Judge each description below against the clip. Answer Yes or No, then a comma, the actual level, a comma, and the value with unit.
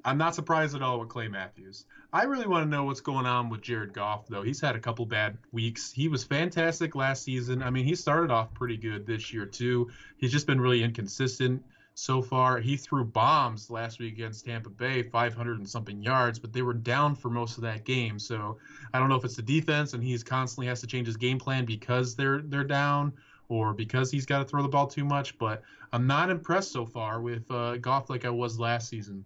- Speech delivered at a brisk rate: Yes, fast, 235 wpm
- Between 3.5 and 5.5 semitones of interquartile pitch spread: No, average, 2.9 semitones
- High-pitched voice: No, low, 125 Hz